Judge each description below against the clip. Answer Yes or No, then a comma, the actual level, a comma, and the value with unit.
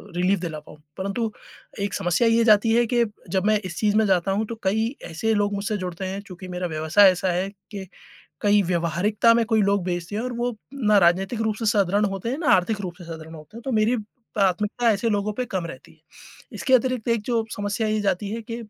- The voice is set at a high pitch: Yes, high, 205 Hz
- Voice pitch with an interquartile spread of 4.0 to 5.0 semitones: No, average, 3.4 semitones